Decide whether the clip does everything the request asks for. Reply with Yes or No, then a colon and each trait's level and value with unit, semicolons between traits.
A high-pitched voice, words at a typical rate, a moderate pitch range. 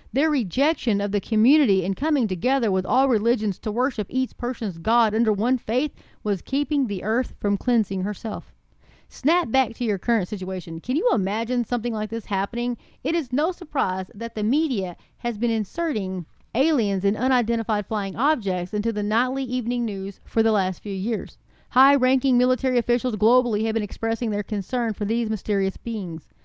Yes: high, 230 Hz; average, 175 wpm; average, 3.6 semitones